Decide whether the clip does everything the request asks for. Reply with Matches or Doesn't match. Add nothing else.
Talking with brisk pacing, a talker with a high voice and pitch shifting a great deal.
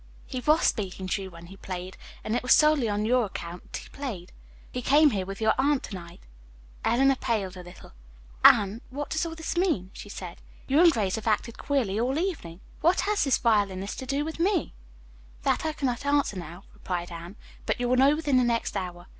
Matches